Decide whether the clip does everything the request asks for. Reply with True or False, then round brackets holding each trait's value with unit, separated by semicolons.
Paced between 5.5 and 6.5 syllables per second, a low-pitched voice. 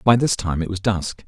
False (5.1 syllables/s; 95 Hz)